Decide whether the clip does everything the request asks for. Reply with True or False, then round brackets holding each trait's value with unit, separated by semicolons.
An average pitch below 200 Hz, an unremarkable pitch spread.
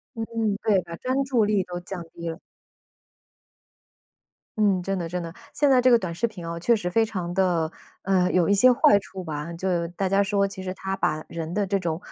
True (190 Hz; 3.4 semitones)